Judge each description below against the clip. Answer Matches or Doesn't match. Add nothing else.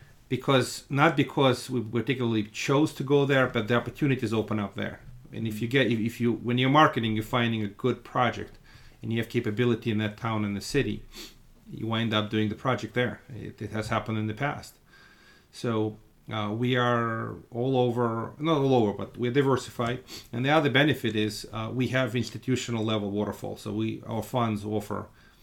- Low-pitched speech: Matches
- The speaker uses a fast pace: Doesn't match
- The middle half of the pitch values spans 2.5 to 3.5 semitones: Matches